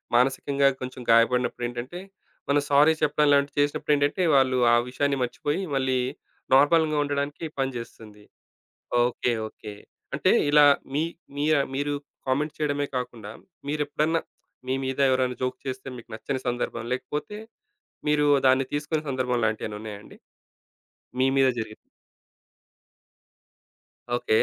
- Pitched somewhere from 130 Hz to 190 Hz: Yes, low, 135 Hz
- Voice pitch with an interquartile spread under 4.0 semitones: Yes, average, 2.8 semitones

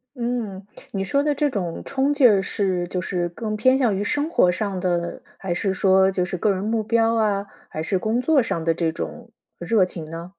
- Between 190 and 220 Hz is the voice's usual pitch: Yes, high, 200 Hz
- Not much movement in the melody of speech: No, average, 4.3 semitones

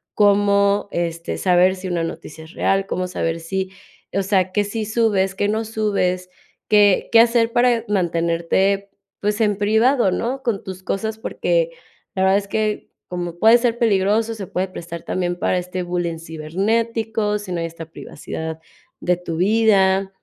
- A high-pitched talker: Yes, high, 195 Hz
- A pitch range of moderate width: Yes, average, 3.5 semitones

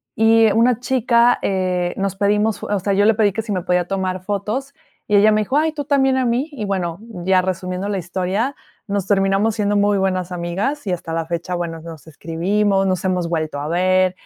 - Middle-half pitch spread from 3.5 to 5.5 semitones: No, average, 3.1 semitones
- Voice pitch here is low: No, high, 195 Hz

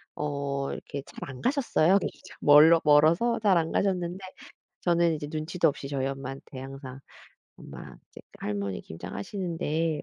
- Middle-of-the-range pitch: Yes, medium, 150 Hz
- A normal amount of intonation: Yes, average, 3.9 semitones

